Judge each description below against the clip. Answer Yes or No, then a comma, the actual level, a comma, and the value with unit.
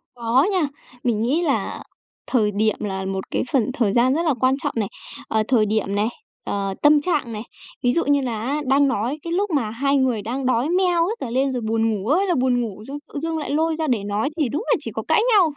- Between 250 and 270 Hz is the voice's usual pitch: Yes, very high, 255 Hz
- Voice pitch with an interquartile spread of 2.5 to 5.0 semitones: No, wide, 5.5 semitones